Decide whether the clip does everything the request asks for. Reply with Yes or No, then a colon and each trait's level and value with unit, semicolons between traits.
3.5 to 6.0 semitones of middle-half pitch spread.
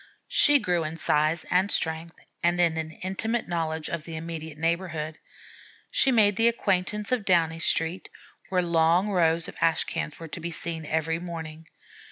No: narrow, 2.4 semitones